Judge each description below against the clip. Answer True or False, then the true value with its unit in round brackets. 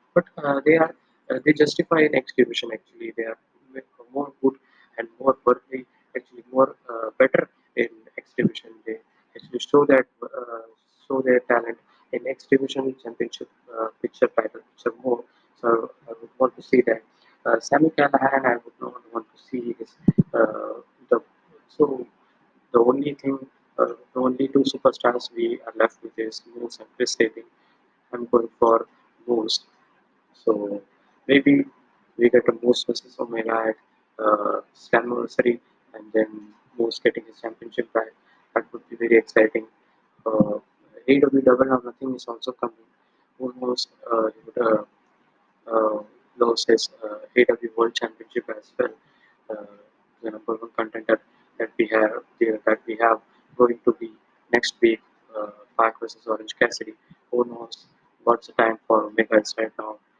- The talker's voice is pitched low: True (120 Hz)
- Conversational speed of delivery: True (155 wpm)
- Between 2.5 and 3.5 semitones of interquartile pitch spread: True (2.9 semitones)